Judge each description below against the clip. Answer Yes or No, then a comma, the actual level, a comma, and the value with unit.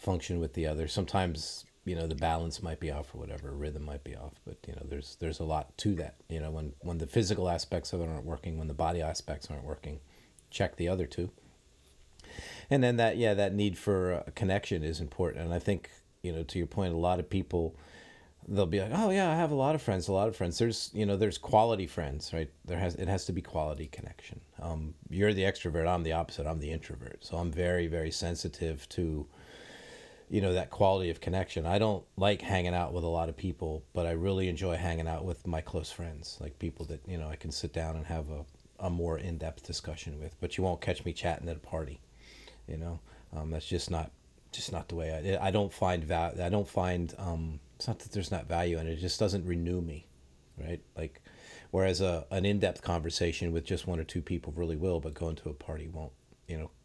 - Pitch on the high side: No, very low, 85 Hz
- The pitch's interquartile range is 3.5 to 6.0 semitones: No, average, 2.8 semitones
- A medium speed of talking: No, fast, 235 wpm